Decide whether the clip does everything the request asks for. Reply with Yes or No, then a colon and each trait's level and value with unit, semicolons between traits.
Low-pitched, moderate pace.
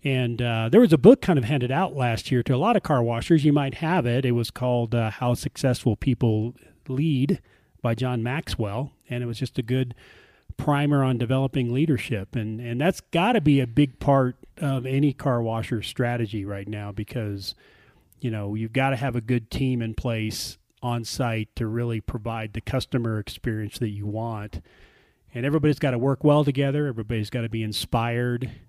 Yes: low, 125 Hz; average, 195 wpm